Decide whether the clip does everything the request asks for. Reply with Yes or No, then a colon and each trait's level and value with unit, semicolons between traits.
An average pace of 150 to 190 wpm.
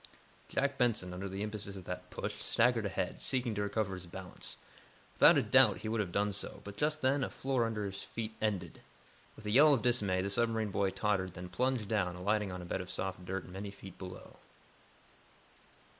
No: fast, 205 wpm